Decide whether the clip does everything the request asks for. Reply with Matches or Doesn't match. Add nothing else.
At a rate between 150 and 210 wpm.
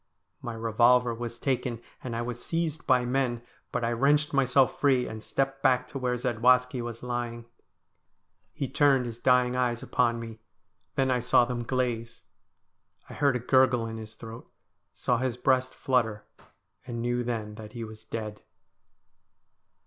Matches